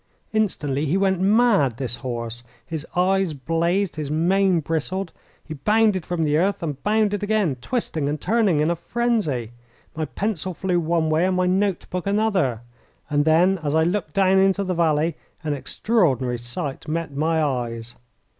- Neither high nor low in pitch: Yes, medium, 165 Hz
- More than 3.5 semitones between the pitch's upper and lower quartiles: Yes, average, 4.7 semitones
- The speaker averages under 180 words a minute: Yes, average, 165 wpm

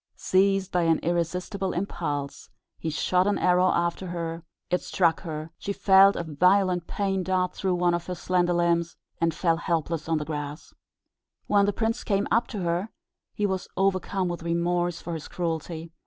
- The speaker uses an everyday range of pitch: No, narrow, 2.3 semitones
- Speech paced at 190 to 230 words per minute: No, average, 175 wpm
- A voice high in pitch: No, medium, 175 Hz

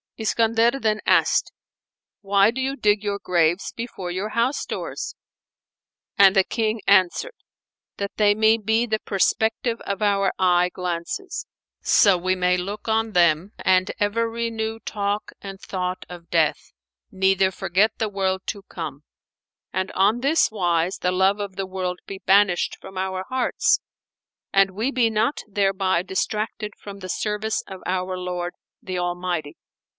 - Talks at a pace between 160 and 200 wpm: No, average, 150 wpm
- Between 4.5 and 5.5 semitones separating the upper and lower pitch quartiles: No, average, 3.0 semitones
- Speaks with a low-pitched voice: No, high, 195 Hz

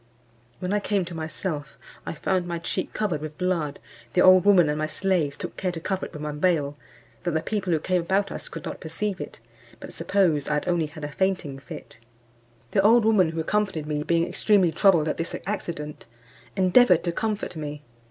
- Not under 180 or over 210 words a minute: Yes, fast, 205 wpm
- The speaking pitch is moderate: Yes, medium, 175 Hz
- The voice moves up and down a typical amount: Yes, average, 3.8 semitones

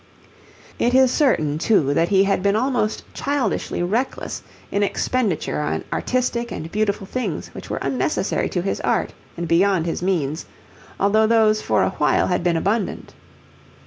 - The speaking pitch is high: Yes, high, 200 Hz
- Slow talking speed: No, average, 155 wpm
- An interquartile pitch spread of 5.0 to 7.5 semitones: Yes, average, 5.3 semitones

